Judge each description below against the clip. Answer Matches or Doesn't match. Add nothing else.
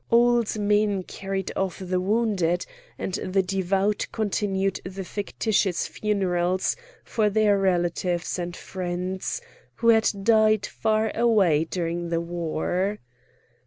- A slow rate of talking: Matches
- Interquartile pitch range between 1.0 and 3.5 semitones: Matches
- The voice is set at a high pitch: Matches